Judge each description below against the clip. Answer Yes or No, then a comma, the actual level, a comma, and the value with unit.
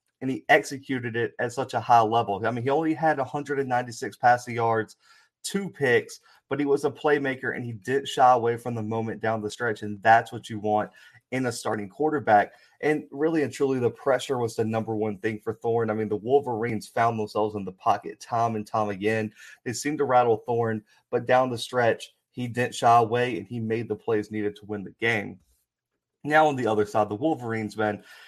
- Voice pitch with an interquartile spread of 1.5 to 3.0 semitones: No, average, 3.6 semitones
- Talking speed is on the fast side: Yes, fast, 215 wpm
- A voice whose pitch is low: Yes, low, 115 Hz